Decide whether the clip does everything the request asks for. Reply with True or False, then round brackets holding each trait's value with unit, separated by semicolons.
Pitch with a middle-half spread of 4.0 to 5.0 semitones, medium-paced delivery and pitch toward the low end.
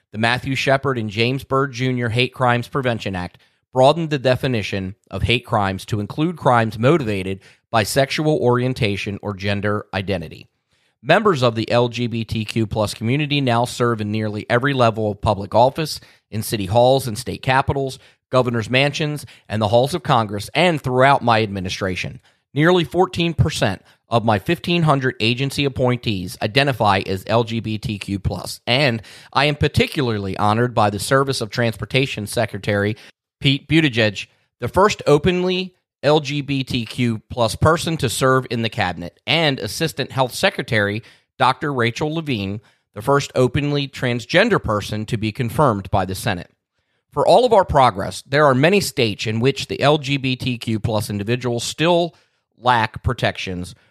True (4.3 semitones; 145 wpm; 120 Hz)